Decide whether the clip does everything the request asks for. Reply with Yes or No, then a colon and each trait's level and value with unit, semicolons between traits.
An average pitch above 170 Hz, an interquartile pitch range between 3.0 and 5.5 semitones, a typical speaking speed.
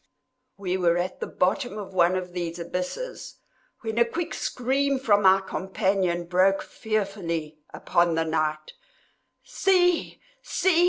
No: high, 190 Hz; average, 5.1 semitones; slow, 130 wpm